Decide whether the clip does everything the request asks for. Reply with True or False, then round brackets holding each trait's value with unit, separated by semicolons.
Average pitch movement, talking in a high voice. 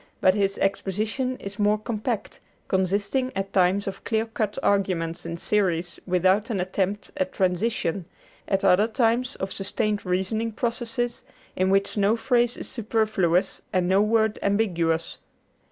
True (3.1 semitones; 200 Hz)